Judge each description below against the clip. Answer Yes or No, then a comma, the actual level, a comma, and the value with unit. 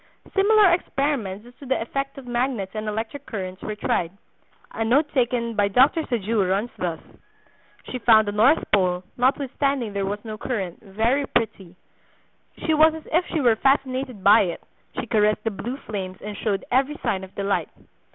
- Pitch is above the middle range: Yes, high, 230 Hz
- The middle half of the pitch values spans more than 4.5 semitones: Yes, average, 5.2 semitones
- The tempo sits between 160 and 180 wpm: Yes, average, 175 wpm